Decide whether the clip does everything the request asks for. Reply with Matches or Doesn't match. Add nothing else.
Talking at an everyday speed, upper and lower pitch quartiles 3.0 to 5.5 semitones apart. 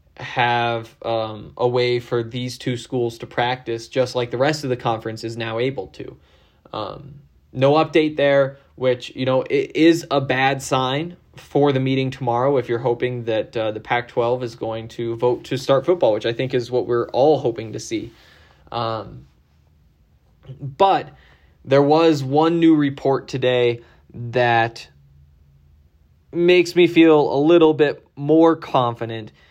Matches